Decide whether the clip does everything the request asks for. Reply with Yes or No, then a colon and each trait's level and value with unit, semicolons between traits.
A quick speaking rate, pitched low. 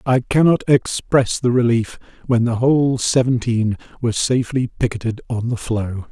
No: average, 145 wpm; low, 120 Hz